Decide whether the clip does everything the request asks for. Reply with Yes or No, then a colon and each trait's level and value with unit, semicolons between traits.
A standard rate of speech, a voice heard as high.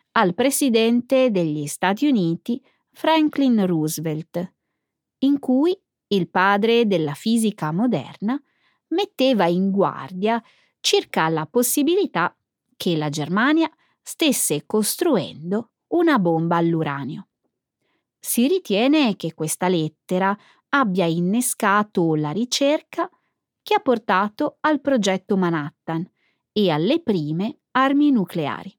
No: slow, 100 wpm; high, 210 Hz